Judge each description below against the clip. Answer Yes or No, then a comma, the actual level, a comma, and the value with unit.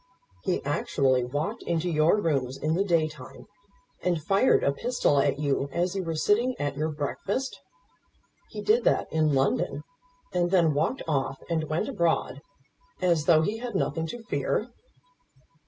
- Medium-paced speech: Yes, average, 160 wpm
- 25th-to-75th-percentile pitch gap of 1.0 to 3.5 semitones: No, average, 4.9 semitones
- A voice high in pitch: No, medium, 160 Hz